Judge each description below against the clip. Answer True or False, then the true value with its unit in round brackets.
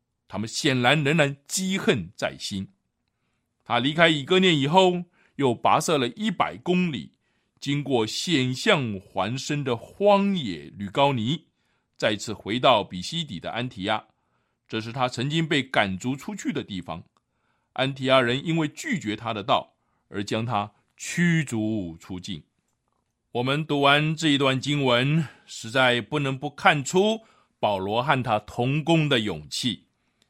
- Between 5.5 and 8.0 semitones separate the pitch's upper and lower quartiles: True (6.4 semitones)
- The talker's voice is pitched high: False (135 Hz)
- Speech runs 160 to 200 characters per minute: False (210 characters per minute)